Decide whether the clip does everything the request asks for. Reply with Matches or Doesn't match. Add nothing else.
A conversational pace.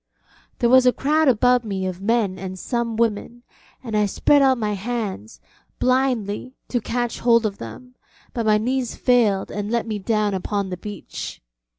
Matches